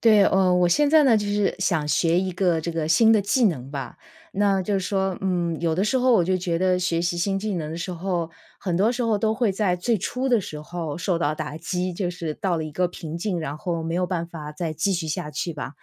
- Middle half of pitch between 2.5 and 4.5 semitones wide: Yes, average, 3.2 semitones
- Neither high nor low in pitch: Yes, medium, 180 Hz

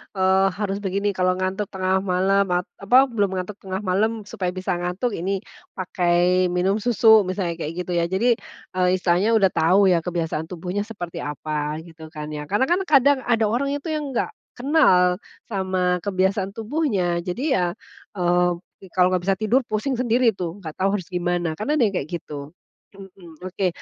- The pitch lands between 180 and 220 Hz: Yes, high, 190 Hz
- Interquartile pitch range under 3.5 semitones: Yes, average, 2.9 semitones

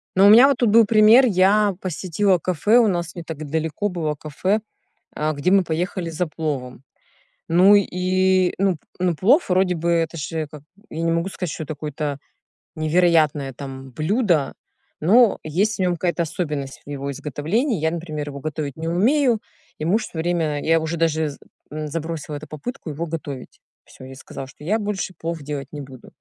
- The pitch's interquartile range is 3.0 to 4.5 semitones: Yes, average, 3.9 semitones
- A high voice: No, medium, 165 Hz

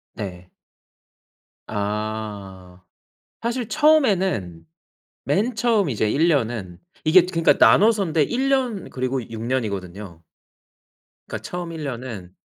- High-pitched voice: No, low, 130 Hz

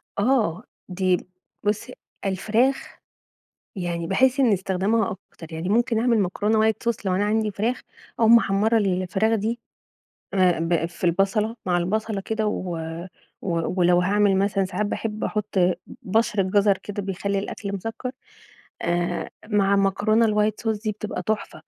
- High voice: Yes, high, 200 Hz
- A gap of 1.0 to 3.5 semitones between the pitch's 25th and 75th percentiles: Yes, average, 2.9 semitones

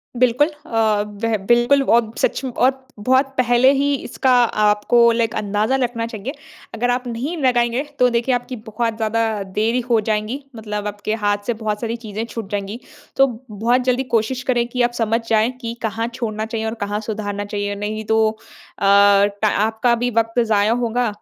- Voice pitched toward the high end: Yes, high, 230 Hz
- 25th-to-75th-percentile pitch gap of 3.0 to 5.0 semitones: No, narrow, 2.5 semitones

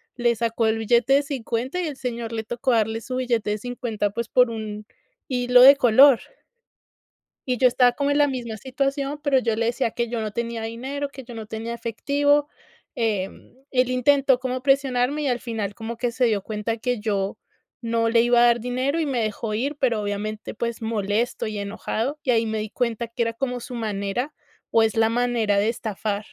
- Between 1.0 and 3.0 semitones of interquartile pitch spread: Yes, narrow, 2.5 semitones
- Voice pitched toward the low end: No, high, 235 Hz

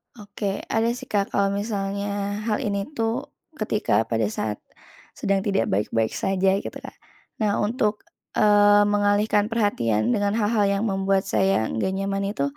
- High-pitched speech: Yes, high, 200 Hz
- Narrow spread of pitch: Yes, narrow, 1.3 semitones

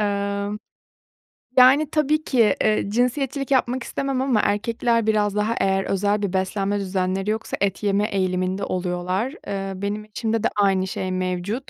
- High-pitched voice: Yes, high, 205 Hz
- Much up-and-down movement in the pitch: No, average, 3.3 semitones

